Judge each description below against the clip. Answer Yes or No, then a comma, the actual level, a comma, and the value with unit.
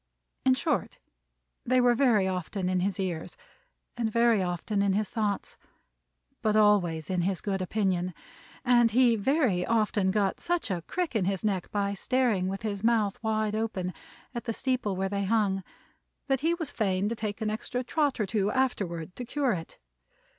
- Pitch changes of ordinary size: Yes, average, 3.8 semitones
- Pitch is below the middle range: No, high, 210 Hz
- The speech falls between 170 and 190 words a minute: Yes, average, 175 wpm